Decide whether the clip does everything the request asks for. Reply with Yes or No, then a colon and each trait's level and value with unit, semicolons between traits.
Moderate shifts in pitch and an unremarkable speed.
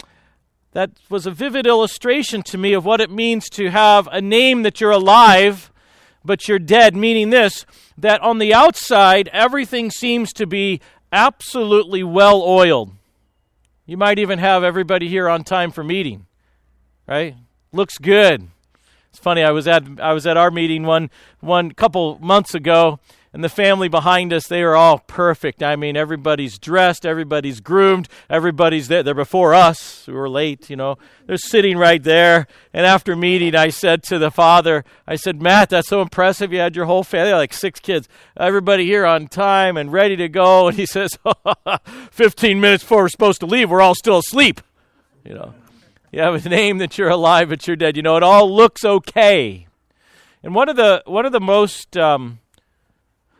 Yes: average, 4.0 semitones; average, 180 wpm